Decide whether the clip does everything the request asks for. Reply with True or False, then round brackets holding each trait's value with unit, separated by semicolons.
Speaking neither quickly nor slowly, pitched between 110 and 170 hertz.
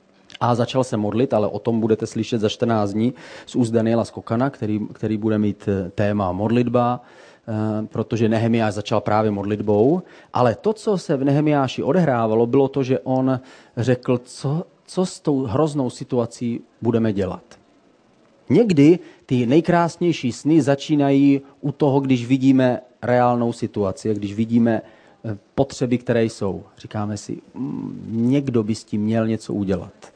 True (145 wpm; 120 Hz)